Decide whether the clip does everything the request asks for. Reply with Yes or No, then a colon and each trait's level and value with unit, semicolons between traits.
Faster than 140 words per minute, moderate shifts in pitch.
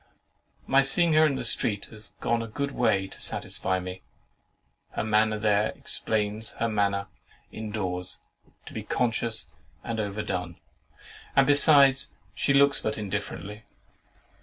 No: slow, 135 wpm; average, 4.4 semitones